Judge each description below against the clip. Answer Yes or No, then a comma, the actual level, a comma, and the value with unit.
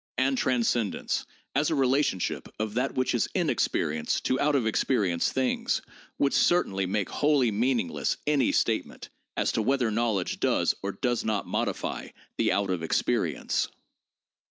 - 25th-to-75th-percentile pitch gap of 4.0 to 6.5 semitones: Yes, average, 4.9 semitones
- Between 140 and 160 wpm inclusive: Yes, average, 150 wpm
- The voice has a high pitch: No, low, 120 Hz